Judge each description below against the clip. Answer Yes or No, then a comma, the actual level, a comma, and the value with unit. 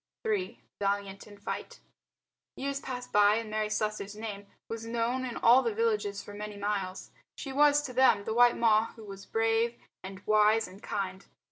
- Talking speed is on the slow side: No, average, 175 wpm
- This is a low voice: No, high, 215 Hz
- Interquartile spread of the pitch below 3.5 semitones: Yes, average, 2.7 semitones